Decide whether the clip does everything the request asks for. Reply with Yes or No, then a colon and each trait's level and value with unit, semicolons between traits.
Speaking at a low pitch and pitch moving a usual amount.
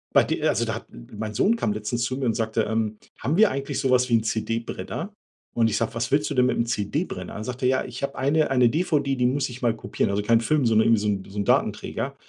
Yes: low, 120 Hz; average, 3.6 semitones